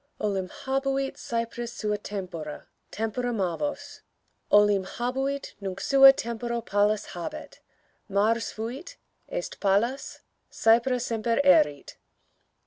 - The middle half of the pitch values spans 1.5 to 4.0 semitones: No, average, 4.6 semitones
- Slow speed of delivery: Yes, slow, 100 wpm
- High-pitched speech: Yes, high, 230 Hz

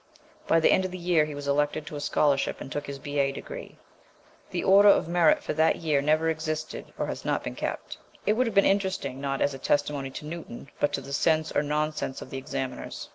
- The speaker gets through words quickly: Yes, fast, 235 wpm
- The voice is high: No, medium, 150 Hz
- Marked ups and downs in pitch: No, average, 2.8 semitones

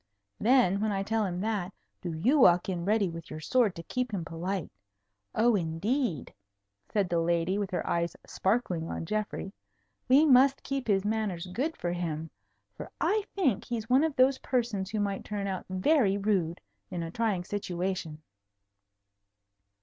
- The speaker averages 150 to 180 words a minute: Yes, average, 165 wpm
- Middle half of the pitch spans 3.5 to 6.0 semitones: Yes, average, 5.2 semitones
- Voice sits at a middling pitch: No, high, 200 Hz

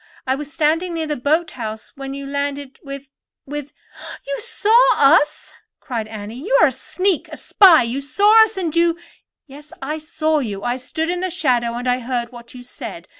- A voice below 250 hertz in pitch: No, very high, 285 Hz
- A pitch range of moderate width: Yes, average, 4.6 semitones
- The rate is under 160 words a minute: No, average, 190 wpm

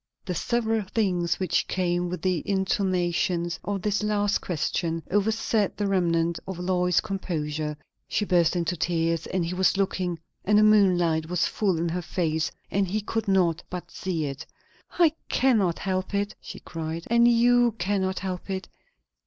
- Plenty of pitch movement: No, average, 3.1 semitones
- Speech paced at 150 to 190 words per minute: Yes, average, 160 wpm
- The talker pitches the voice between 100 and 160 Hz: No, medium, 185 Hz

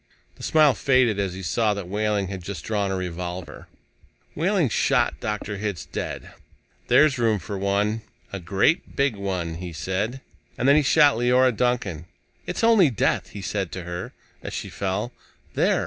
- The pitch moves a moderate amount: Yes, average, 5.0 semitones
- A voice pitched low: Yes, low, 105 Hz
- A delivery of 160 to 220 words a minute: Yes, average, 170 wpm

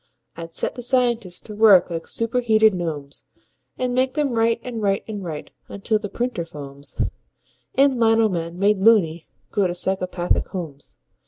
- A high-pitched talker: Yes, high, 205 Hz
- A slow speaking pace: No, average, 160 wpm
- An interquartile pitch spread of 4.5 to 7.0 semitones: Yes, average, 5.0 semitones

